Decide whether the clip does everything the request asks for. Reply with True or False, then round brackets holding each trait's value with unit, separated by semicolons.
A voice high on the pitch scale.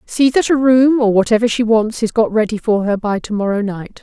True (225 Hz)